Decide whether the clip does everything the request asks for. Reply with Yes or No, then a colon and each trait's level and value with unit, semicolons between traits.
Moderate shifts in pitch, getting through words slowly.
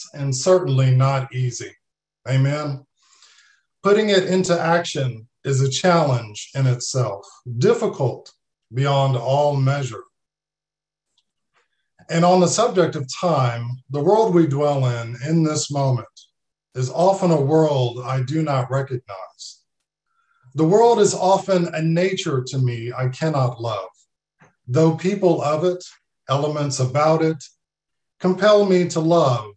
Yes: average, 5.0 semitones; slow, 125 wpm